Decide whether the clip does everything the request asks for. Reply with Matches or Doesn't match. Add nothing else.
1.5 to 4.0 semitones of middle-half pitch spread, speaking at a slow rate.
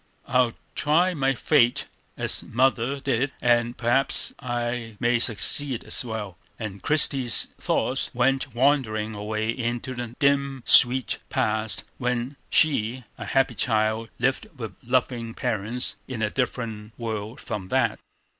Matches